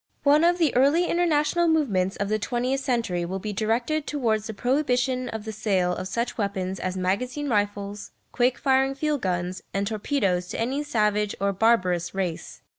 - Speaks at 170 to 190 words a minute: Yes, average, 175 wpm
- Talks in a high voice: Yes, high, 225 Hz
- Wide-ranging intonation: Yes, wide, 5.7 semitones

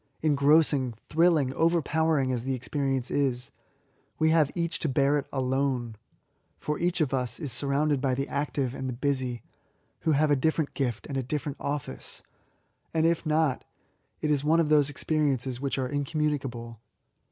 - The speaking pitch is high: No, medium, 140 Hz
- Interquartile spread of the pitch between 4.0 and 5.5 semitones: No, average, 2.9 semitones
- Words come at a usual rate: Yes, average, 165 wpm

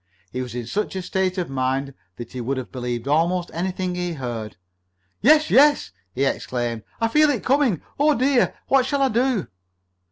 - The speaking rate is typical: Yes, average, 185 wpm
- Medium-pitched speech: Yes, medium, 180 Hz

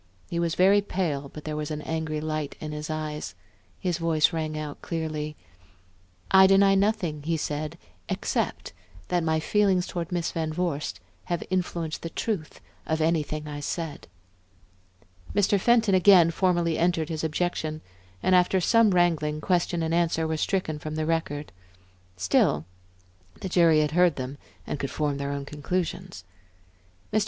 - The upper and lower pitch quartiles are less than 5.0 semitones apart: Yes, average, 2.8 semitones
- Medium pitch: Yes, medium, 160 Hz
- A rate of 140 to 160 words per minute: Yes, average, 155 wpm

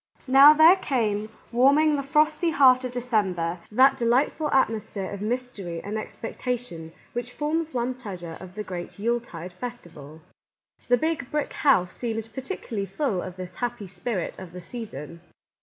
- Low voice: No, high, 235 Hz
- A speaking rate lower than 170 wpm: Yes, average, 155 wpm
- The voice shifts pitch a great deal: Yes, wide, 6.1 semitones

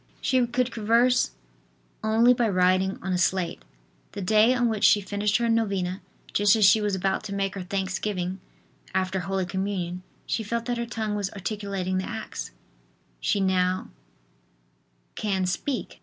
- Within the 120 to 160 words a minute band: Yes, average, 155 wpm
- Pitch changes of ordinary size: Yes, average, 3.0 semitones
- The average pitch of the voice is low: No, high, 200 Hz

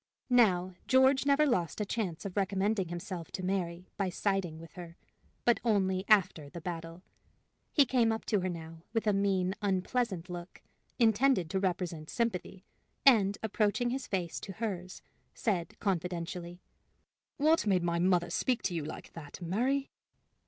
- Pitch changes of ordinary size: Yes, average, 4.2 semitones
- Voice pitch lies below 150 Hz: No, high, 190 Hz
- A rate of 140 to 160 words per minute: Yes, average, 155 wpm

